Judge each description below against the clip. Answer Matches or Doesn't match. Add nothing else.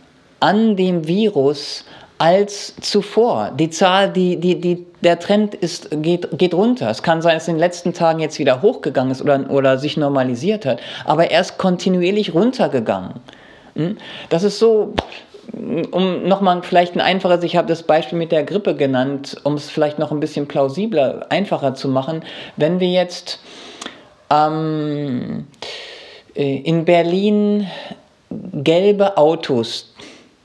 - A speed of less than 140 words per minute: Doesn't match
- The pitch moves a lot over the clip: Doesn't match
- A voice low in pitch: Doesn't match